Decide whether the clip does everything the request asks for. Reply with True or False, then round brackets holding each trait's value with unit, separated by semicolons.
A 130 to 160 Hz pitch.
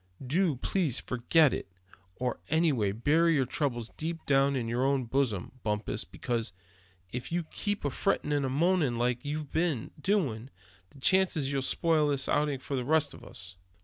True (140 Hz)